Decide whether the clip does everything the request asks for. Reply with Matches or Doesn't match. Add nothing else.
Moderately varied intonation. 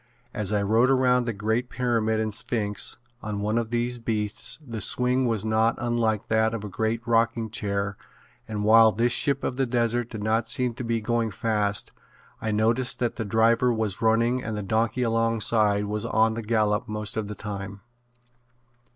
Doesn't match